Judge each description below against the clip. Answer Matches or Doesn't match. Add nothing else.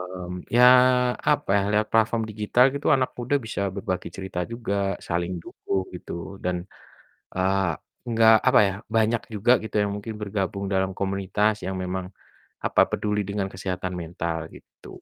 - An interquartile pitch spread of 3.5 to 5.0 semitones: Doesn't match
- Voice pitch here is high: Doesn't match